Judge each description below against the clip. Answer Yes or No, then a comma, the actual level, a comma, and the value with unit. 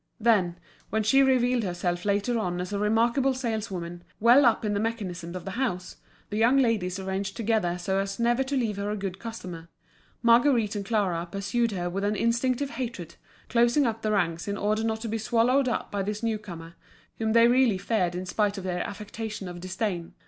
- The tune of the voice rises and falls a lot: No, average, 3.9 semitones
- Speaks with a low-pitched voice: No, high, 210 Hz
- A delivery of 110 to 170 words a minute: No, average, 200 wpm